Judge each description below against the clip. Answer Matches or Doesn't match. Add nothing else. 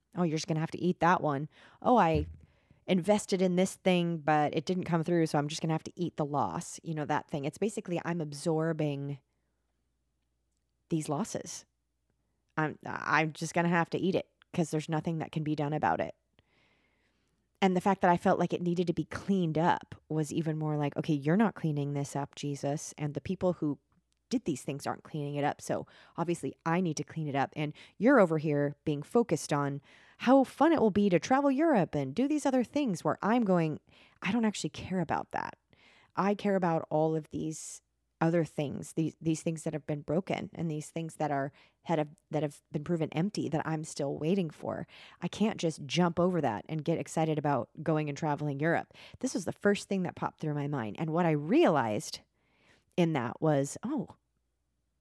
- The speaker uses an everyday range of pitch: Matches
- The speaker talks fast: Matches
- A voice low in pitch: Doesn't match